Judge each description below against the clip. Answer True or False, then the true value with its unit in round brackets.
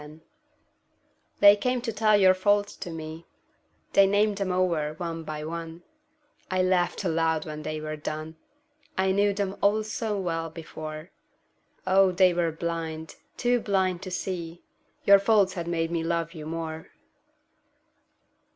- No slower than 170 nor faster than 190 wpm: False (150 wpm)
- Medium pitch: True (175 Hz)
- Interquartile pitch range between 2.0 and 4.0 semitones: True (3.4 semitones)